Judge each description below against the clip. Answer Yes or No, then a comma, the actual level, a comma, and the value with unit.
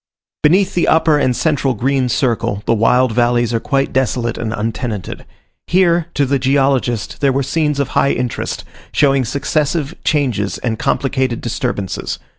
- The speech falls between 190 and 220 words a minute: No, average, 150 wpm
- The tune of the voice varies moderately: Yes, average, 3.3 semitones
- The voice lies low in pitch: Yes, low, 130 Hz